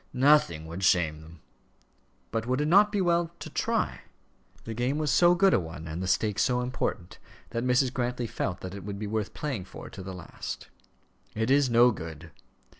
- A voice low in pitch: Yes, low, 115 Hz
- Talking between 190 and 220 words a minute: Yes, average, 195 wpm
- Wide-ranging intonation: Yes, wide, 6.8 semitones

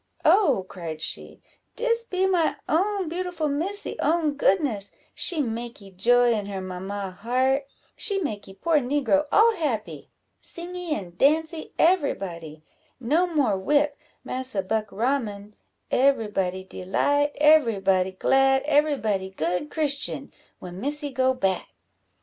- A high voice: Yes, very high, 265 Hz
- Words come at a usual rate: No, slow, 130 wpm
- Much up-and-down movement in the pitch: Yes, wide, 7.7 semitones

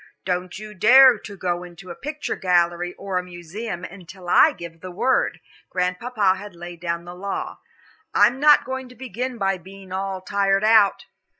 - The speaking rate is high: No, average, 175 wpm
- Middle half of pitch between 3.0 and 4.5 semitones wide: Yes, average, 3.3 semitones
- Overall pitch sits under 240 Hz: Yes, high, 190 Hz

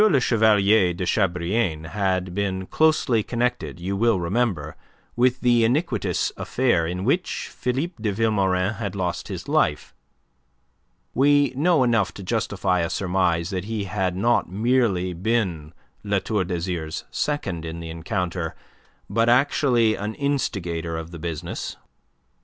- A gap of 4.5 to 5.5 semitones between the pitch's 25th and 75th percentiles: Yes, average, 5.1 semitones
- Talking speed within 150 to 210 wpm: No, slow, 135 wpm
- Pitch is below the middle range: Yes, low, 100 Hz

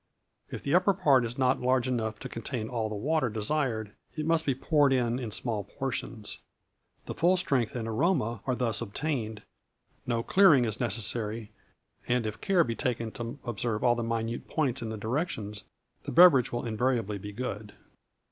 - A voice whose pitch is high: No, low, 120 Hz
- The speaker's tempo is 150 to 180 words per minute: Yes, average, 175 wpm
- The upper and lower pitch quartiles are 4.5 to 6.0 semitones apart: No, average, 3.4 semitones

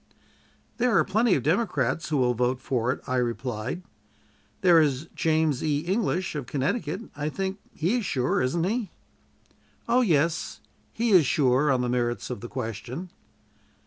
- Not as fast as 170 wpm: Yes, average, 160 wpm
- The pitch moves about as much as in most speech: No, wide, 6.5 semitones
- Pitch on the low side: No, medium, 150 Hz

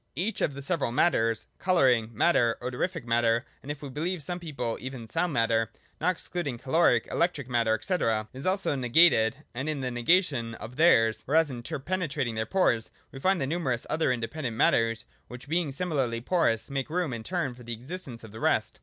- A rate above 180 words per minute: Yes, average, 195 wpm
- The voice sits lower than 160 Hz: Yes, low, 135 Hz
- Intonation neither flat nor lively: No, wide, 6.1 semitones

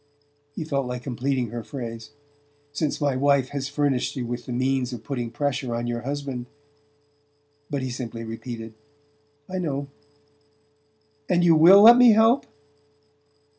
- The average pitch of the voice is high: No, low, 135 Hz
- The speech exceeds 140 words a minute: Yes, average, 150 wpm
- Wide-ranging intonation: No, average, 3.1 semitones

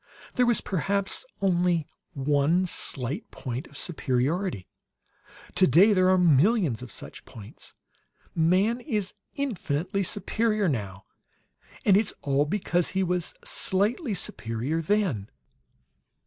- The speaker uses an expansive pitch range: Yes, wide, 6.0 semitones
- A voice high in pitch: No, medium, 180 Hz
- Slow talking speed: Yes, slow, 110 wpm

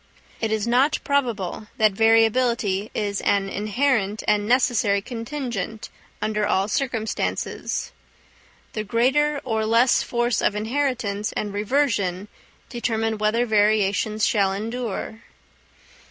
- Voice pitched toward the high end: Yes, high, 220 Hz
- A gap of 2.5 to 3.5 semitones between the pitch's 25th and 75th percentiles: Yes, average, 2.8 semitones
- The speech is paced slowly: Yes, slow, 110 wpm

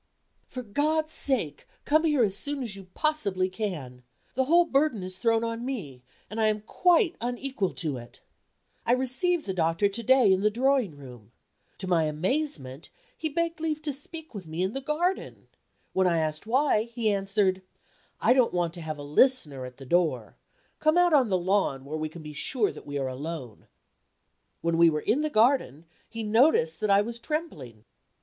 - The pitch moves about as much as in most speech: No, wide, 8.8 semitones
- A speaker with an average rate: Yes, average, 190 wpm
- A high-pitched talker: Yes, high, 210 Hz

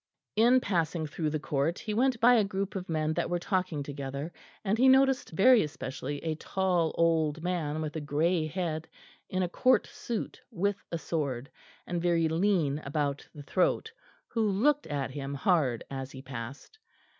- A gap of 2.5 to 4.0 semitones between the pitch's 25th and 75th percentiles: No, average, 4.9 semitones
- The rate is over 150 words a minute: Yes, average, 175 wpm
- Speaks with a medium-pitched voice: Yes, medium, 165 Hz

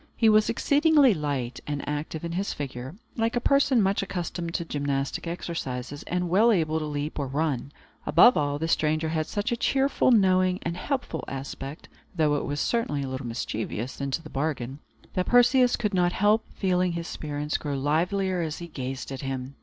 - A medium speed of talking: Yes, average, 185 wpm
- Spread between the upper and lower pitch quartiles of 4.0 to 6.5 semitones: Yes, wide, 5.4 semitones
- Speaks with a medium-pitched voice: Yes, medium, 160 Hz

